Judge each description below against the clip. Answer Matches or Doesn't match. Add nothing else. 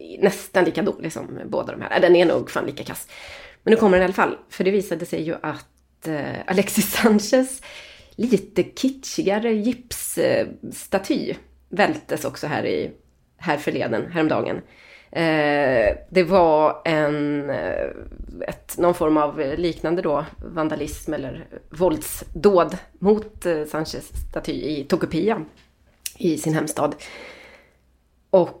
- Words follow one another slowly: Matches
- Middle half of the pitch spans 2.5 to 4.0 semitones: Doesn't match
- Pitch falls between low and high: Matches